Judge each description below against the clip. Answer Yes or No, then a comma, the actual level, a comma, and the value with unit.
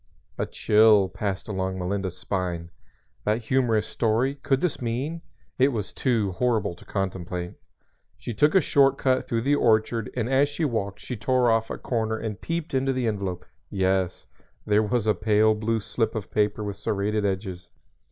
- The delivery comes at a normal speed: Yes, average, 170 wpm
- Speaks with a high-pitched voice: No, low, 110 Hz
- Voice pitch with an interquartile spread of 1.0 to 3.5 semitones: No, average, 4.0 semitones